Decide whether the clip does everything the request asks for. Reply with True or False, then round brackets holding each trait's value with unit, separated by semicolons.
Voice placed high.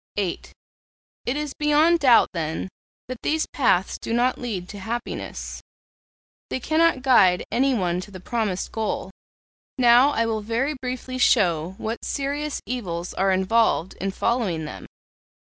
True (230 Hz)